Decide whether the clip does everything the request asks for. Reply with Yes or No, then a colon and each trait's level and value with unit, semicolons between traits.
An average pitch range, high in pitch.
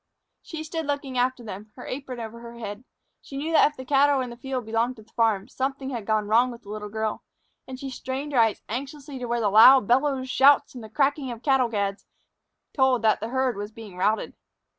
Yes: average, 3.5 semitones; very high, 250 Hz